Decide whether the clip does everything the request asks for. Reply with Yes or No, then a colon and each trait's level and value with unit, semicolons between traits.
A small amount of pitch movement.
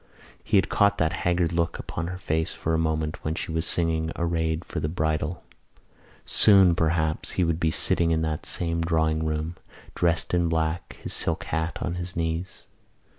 Yes: narrow, 1.4 semitones